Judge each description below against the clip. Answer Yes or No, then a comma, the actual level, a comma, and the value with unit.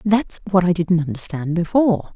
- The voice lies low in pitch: No, medium, 180 Hz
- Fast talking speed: No, average, 165 wpm